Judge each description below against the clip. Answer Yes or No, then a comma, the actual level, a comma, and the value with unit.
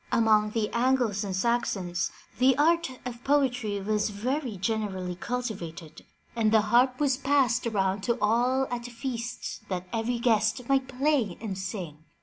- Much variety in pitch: No, average, 3.8 semitones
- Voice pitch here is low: No, high, 230 Hz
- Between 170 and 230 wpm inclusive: No, average, 145 wpm